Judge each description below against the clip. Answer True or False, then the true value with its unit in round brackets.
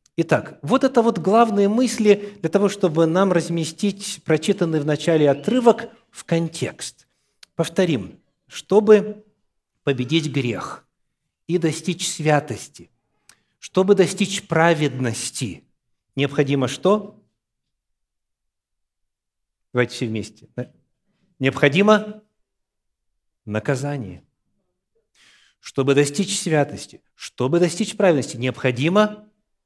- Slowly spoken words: True (85 wpm)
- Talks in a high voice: False (160 Hz)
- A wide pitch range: True (7.7 semitones)